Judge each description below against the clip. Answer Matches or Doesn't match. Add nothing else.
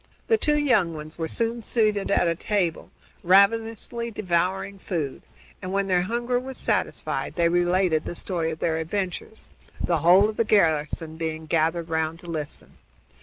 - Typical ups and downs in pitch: Matches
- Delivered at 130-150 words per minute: Doesn't match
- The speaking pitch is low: Doesn't match